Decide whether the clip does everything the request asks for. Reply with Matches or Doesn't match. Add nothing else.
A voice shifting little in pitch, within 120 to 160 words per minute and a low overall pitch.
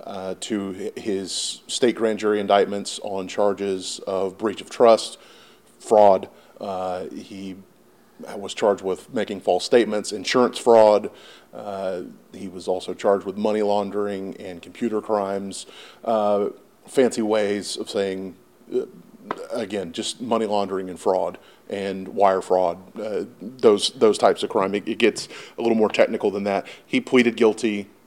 Matches